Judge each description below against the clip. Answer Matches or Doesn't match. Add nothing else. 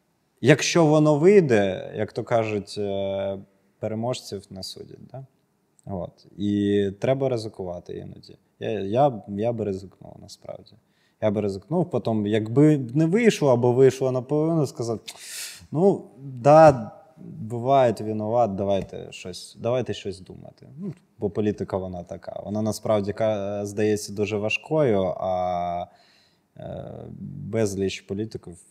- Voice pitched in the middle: Doesn't match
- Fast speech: Doesn't match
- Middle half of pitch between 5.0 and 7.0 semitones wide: Matches